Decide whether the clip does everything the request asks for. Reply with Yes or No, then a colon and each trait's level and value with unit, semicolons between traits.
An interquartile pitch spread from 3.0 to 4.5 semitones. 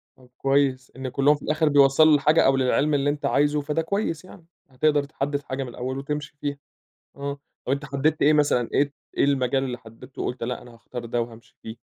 No: narrow, 2.4 semitones